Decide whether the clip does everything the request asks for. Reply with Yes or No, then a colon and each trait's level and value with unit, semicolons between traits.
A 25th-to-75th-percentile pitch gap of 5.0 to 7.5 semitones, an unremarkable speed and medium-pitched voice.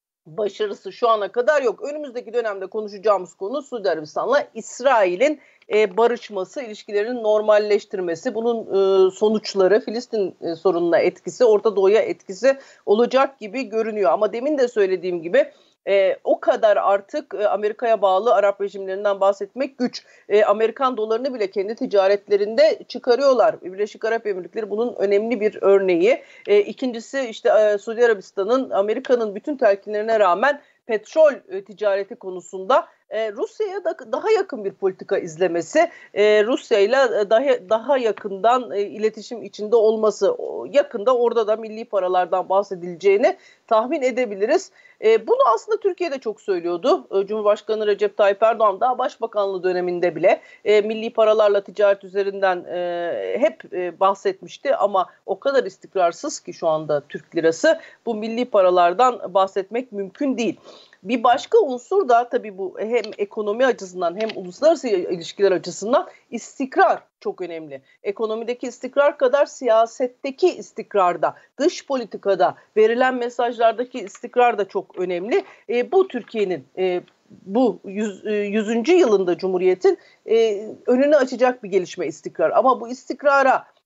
No: average, 5.3 semitones; average, 130 wpm; high, 220 Hz